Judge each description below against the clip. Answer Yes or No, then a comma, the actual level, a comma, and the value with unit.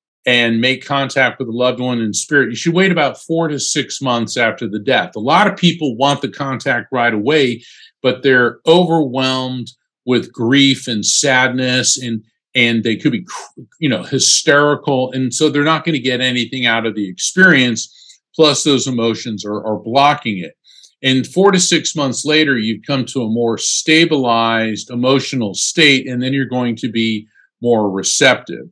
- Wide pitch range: No, average, 3.7 semitones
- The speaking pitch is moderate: No, low, 130 Hz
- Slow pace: No, average, 180 wpm